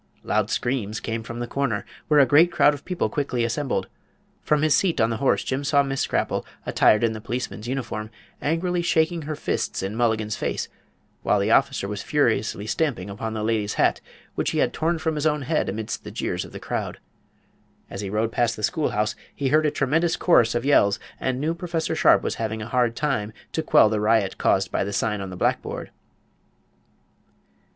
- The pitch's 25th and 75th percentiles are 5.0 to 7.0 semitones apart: Yes, wide, 5.6 semitones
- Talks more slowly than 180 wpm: No, average, 200 wpm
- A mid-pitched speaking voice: No, low, 120 Hz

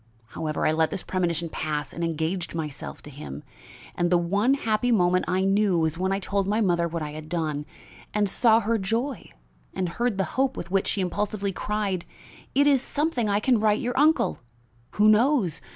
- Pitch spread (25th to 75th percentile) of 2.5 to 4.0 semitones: No, average, 4.5 semitones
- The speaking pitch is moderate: No, high, 195 Hz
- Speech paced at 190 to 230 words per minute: Yes, average, 195 wpm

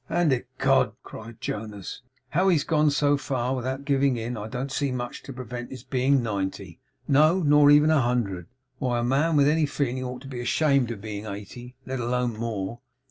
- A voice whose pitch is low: Yes, low, 125 Hz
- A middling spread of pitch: Yes, average, 3.3 semitones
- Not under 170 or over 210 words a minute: Yes, average, 190 wpm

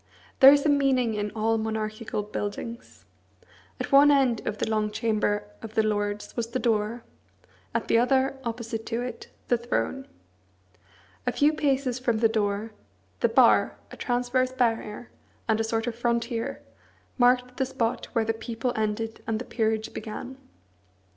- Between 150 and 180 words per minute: Yes, average, 160 wpm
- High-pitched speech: Yes, high, 230 Hz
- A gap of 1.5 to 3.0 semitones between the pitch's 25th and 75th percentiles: Yes, narrow, 2.4 semitones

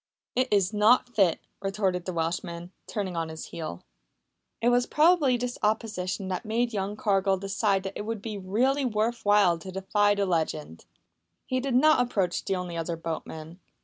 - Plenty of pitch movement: No, average, 4.2 semitones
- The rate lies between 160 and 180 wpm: Yes, average, 175 wpm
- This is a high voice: Yes, high, 200 Hz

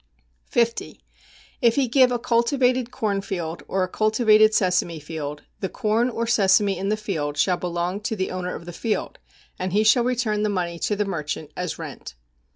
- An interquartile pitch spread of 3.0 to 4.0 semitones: No, average, 4.5 semitones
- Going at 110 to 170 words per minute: No, average, 185 wpm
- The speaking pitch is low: No, high, 205 Hz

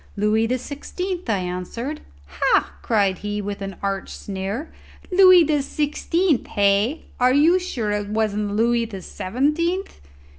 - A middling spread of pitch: No, wide, 6.9 semitones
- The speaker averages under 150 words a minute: Yes, average, 140 wpm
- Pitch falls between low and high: No, high, 225 Hz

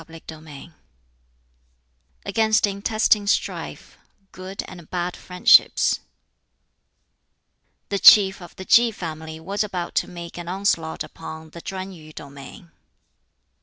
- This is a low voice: No, medium, 180 Hz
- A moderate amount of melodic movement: Yes, average, 3.6 semitones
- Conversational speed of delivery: No, slow, 115 wpm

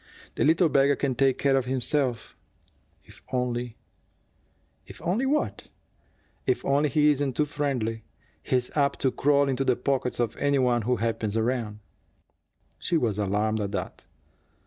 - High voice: No, low, 130 Hz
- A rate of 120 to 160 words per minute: Yes, average, 155 wpm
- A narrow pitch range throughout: No, average, 3.4 semitones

